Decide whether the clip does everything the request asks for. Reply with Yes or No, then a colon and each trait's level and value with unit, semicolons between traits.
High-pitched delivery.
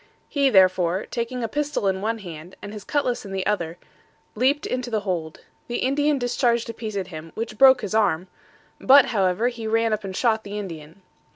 Yes: high, 215 Hz